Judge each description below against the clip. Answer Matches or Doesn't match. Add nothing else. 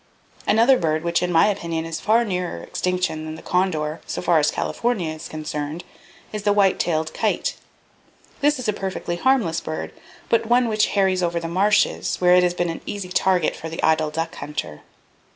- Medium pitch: Matches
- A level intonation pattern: Doesn't match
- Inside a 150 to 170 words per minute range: Doesn't match